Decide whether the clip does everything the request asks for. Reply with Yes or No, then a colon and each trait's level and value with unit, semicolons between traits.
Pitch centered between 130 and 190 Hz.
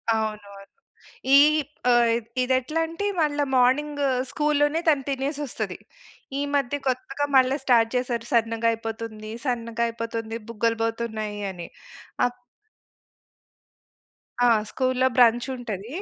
No: high, 240 Hz